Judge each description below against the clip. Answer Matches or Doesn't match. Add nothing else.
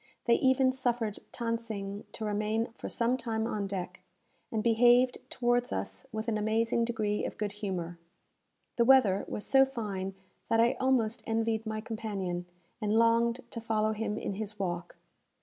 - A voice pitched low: Doesn't match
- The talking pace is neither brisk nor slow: Matches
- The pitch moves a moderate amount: Doesn't match